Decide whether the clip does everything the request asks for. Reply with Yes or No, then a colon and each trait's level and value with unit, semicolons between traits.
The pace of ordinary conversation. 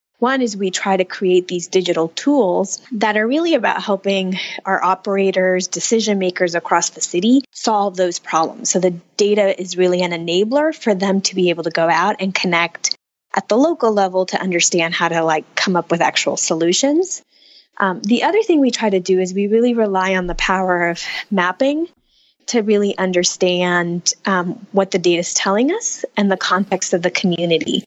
Yes: average, 190 wpm